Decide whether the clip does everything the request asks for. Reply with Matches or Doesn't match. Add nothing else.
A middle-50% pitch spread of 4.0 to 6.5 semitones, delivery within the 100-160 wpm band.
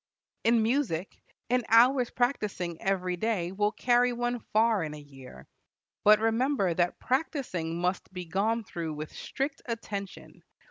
Matches